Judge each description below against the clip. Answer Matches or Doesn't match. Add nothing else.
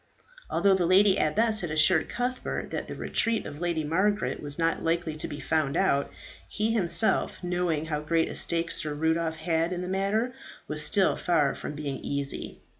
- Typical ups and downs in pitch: Matches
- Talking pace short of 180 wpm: Doesn't match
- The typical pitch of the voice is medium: Matches